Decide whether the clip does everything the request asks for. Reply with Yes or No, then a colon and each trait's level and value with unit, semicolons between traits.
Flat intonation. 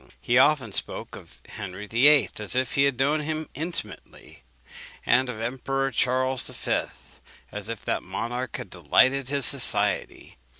No: average, 3.3 semitones